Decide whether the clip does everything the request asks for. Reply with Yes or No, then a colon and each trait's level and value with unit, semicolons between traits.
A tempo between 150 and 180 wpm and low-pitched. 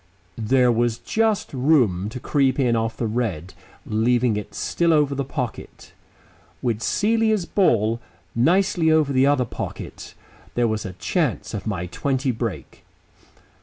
No: average, 140 wpm; low, 125 Hz